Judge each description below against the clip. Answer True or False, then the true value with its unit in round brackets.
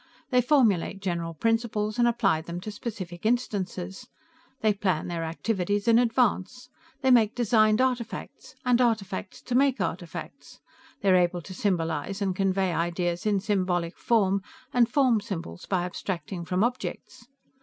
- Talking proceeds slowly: False (145 wpm)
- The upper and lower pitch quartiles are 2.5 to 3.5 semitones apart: False (4.7 semitones)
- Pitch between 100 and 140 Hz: False (200 Hz)